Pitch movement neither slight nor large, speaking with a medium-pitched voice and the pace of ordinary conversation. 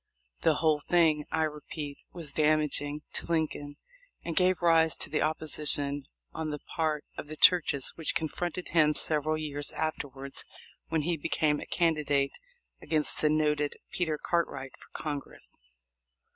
No: narrow, 1.6 semitones; medium, 155 Hz; average, 145 wpm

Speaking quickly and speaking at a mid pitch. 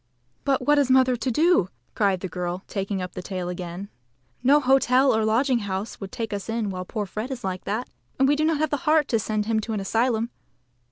No: fast, 225 wpm; high, 225 Hz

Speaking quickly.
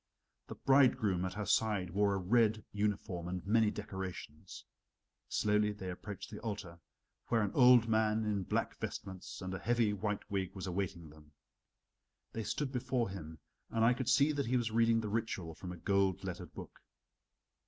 No: average, 175 wpm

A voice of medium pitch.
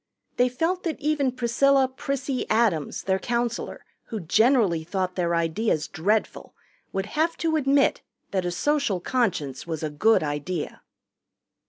No: high, 225 Hz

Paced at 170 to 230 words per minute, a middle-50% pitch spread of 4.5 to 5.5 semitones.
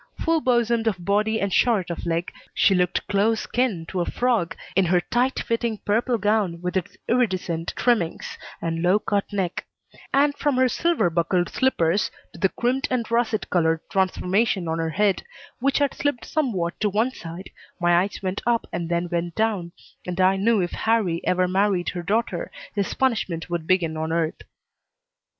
Yes: average, 175 wpm; average, 5.0 semitones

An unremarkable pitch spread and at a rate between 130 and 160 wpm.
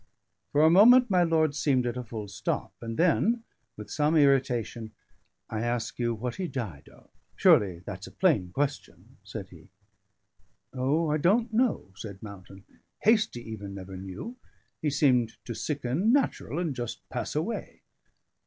No: wide, 7.2 semitones; average, 155 wpm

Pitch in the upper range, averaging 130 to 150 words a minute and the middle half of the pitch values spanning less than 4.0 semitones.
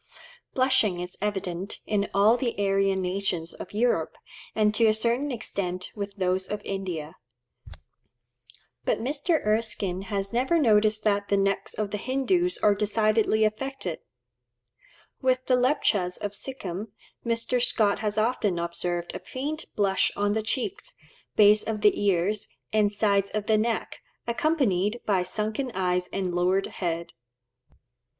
Yes: high, 210 Hz; average, 140 wpm; average, 3.3 semitones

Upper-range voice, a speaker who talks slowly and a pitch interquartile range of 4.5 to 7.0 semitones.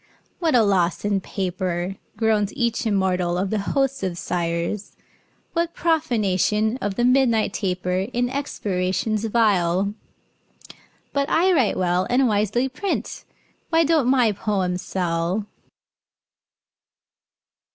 Yes: high, 210 Hz; slow, 115 wpm; average, 5.2 semitones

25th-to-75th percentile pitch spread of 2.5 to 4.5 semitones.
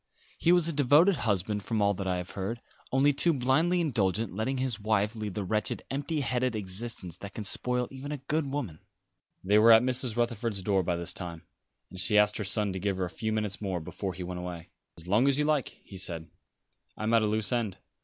No: average, 5.3 semitones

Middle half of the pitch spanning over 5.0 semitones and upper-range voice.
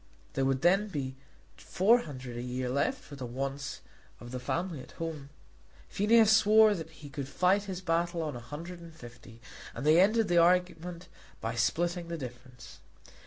No: wide, 5.5 semitones; medium, 165 Hz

